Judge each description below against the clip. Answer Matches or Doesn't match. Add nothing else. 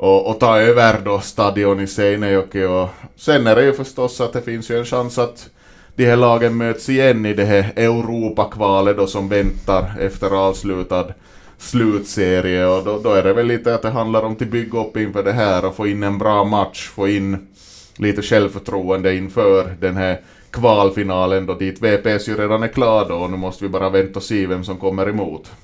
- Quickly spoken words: Matches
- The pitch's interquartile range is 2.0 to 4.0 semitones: Matches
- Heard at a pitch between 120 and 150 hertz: Doesn't match